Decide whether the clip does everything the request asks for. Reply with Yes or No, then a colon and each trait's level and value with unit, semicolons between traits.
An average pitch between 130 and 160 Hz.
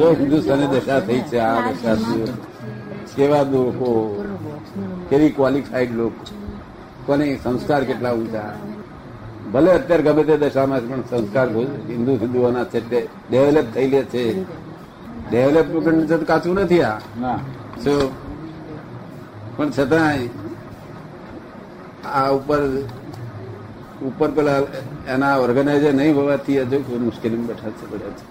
Yes: low, 135 Hz